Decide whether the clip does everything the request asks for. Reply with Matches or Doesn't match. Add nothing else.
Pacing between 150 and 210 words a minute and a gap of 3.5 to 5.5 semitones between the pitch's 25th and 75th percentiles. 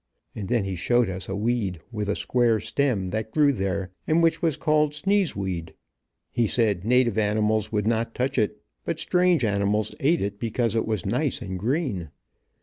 Matches